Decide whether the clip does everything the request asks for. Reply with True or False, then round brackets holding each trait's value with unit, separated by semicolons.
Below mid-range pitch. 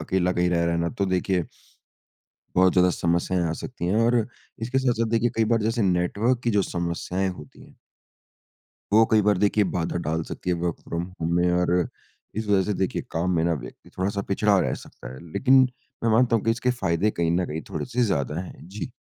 True (95 Hz)